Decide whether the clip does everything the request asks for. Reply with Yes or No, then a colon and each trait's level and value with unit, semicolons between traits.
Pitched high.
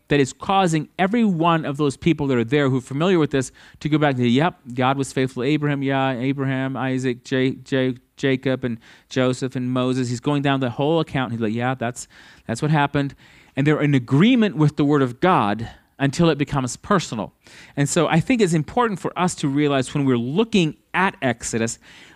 No: medium, 140 Hz